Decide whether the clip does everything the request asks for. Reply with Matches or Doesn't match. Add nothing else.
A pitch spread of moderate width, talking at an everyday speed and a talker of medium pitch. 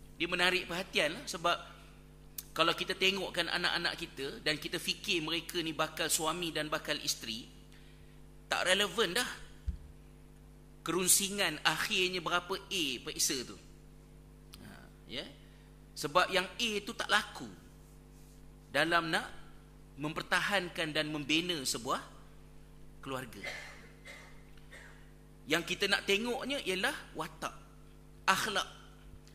Matches